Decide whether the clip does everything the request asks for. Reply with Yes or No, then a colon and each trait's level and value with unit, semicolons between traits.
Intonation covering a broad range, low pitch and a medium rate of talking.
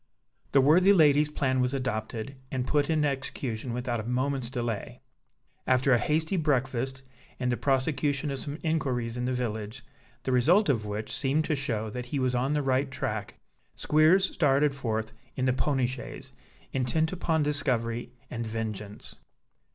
No: average, 3.2 semitones; low, 130 Hz; average, 160 wpm